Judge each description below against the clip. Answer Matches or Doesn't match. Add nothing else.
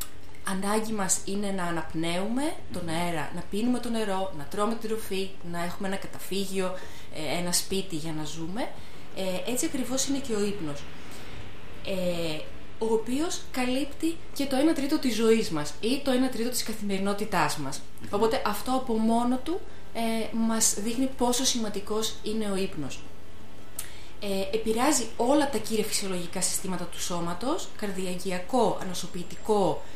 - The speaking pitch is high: Matches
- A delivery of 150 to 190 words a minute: Doesn't match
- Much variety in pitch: Doesn't match